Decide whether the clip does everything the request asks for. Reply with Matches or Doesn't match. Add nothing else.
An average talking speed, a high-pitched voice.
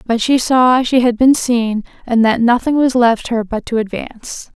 Doesn't match